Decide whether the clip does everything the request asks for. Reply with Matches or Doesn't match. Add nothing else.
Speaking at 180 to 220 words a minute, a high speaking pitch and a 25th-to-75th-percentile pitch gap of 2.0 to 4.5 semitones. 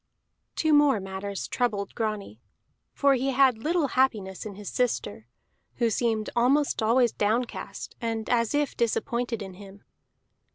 Doesn't match